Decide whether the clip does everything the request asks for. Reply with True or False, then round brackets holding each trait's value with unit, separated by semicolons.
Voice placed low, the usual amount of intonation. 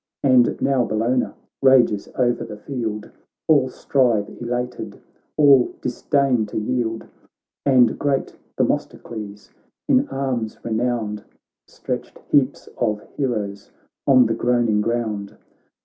True (120 Hz; 3.1 semitones)